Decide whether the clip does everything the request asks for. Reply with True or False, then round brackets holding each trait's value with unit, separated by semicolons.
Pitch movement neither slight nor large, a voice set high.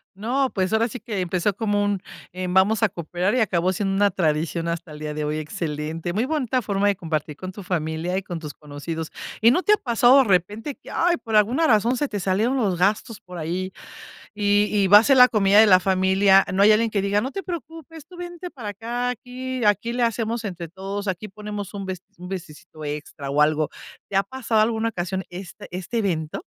True (4.6 semitones; 200 Hz)